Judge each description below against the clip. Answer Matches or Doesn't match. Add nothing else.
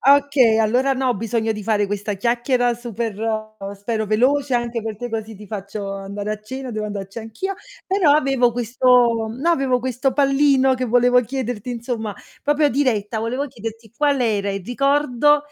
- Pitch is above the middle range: Matches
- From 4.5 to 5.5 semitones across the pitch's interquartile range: Doesn't match